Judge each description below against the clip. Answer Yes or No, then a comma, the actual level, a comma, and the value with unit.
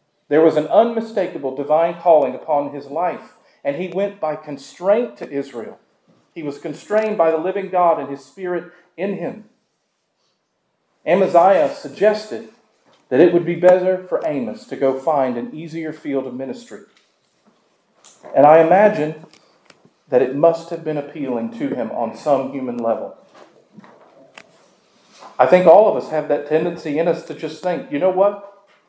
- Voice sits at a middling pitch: Yes, medium, 160 Hz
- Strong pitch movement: No, average, 4.3 semitones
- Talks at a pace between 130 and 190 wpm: Yes, average, 160 wpm